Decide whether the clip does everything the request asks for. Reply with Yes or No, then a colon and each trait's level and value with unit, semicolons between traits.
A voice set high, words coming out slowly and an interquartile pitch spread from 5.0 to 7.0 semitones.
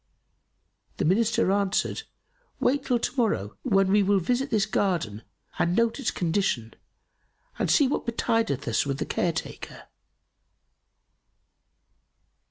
Yes: high, 200 Hz; slow, 125 wpm; wide, 5.5 semitones